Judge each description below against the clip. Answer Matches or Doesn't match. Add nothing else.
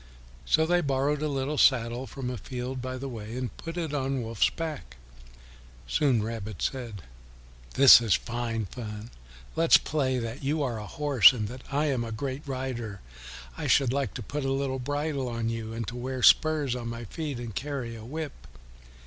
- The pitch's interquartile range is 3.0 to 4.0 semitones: Matches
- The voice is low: Matches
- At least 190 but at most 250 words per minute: Matches